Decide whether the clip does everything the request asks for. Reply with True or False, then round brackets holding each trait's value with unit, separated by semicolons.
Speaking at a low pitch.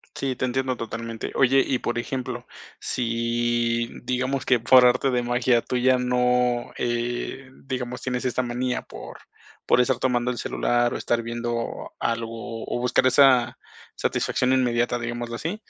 True (120 Hz)